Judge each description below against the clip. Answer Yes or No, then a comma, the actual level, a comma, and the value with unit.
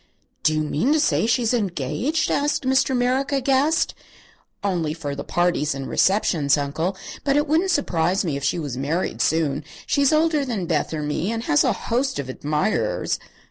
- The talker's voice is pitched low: No, medium, 185 Hz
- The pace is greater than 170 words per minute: Yes, average, 180 wpm